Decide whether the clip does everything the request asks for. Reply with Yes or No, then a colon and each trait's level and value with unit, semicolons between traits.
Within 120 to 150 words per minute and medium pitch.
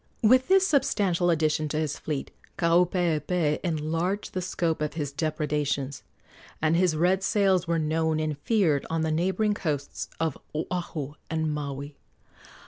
Yes: average, 140 wpm; medium, 160 Hz